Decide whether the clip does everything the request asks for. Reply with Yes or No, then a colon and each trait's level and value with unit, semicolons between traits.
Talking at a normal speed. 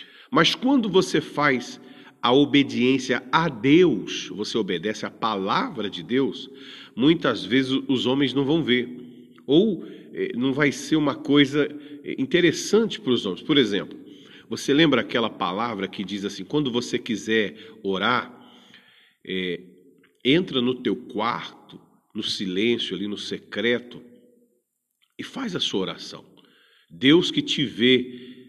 Yes: average, 135 wpm